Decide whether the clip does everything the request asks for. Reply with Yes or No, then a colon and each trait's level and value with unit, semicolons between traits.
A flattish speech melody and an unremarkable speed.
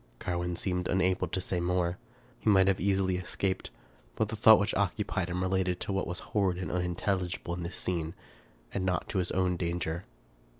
Yes: narrow, 1.4 semitones; average, 185 wpm